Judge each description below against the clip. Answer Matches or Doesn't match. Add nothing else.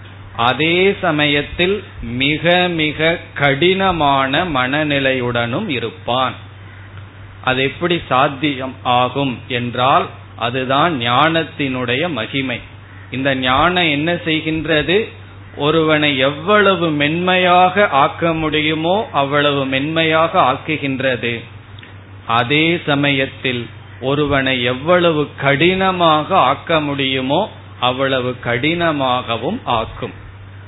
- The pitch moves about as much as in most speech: Matches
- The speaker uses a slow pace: Matches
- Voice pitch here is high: Doesn't match